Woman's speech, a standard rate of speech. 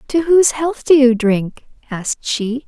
Yes: female; average, 180 wpm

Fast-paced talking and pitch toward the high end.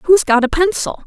Yes: fast, 225 wpm; very high, 320 Hz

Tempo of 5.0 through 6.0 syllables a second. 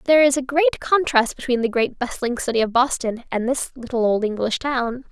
Yes: 5.3 syllables/s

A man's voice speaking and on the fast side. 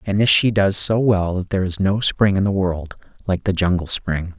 Yes: male; fast, 245 wpm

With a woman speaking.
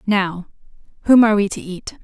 Yes: female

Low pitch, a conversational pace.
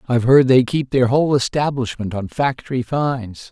Yes: low, 125 Hz; average, 170 wpm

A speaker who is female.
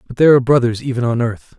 No: male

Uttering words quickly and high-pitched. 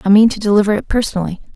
Yes: fast, 230 wpm; high, 205 Hz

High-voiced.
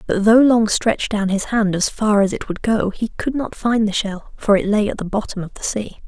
Yes: high, 210 Hz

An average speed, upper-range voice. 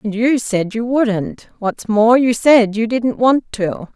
Yes: average, 195 wpm; high, 230 Hz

